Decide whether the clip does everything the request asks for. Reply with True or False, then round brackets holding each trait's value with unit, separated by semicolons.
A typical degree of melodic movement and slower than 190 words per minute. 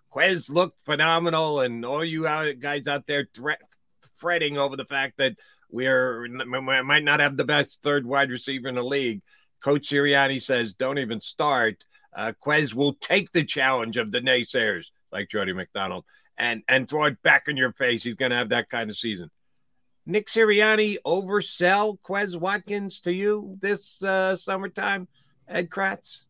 False (6.2 semitones; 170 wpm)